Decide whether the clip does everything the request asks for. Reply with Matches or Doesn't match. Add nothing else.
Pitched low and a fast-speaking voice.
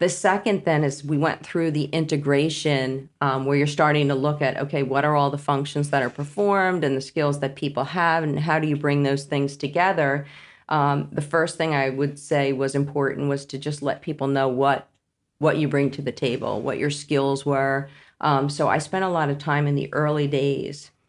Doesn't match